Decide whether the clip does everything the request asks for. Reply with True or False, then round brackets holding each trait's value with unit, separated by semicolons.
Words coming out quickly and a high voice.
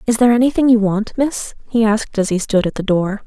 True (260 wpm; 220 Hz)